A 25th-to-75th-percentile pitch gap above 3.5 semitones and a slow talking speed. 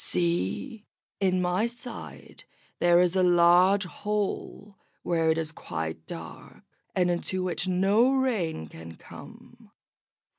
Yes: average, 4.0 semitones; slow, 120 wpm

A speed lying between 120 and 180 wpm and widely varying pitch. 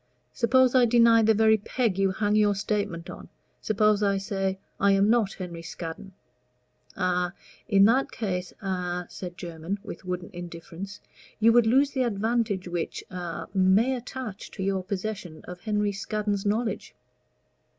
No: average, 150 wpm; average, 3.3 semitones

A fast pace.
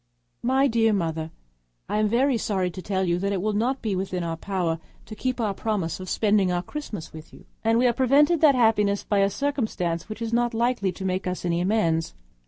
Yes: fast, 215 wpm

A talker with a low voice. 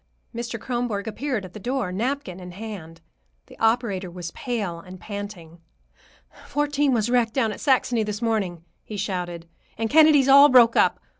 No: high, 220 Hz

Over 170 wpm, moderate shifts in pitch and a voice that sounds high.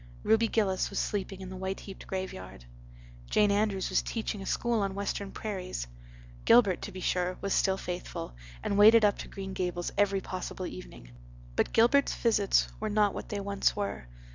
No: average, 180 wpm; narrow, 2.0 semitones; high, 195 Hz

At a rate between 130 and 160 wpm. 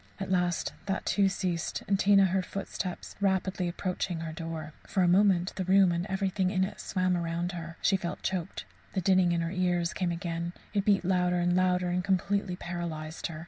No: average, 195 wpm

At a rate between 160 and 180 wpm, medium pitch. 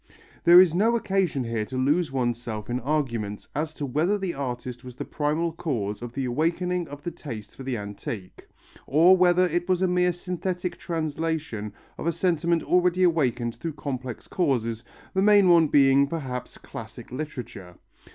Yes: average, 170 wpm; medium, 150 Hz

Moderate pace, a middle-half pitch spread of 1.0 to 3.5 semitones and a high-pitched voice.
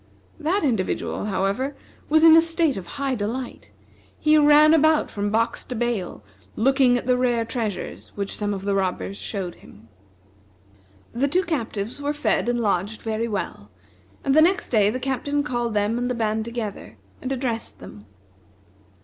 No: average, 165 wpm; wide, 5.5 semitones; high, 240 Hz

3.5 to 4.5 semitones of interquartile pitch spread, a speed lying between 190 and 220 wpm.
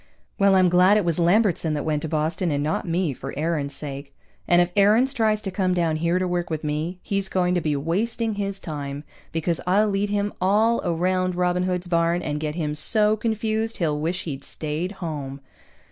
Yes: average, 4.2 semitones; fast, 205 wpm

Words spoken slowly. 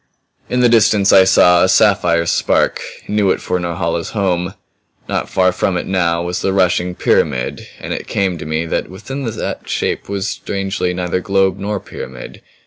No: average, 175 wpm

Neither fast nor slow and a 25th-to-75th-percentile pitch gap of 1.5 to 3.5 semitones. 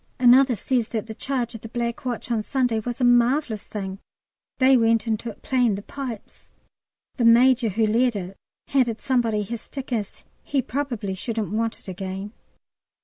Yes: average, 175 wpm; average, 2.8 semitones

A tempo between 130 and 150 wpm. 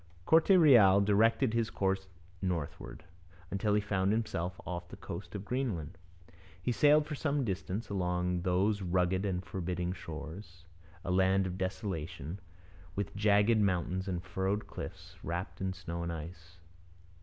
Yes: average, 145 wpm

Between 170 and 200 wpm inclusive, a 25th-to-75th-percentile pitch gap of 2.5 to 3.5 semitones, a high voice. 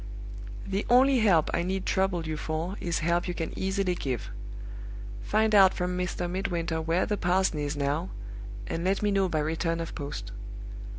No: average, 175 wpm; average, 2.9 semitones; medium, 175 Hz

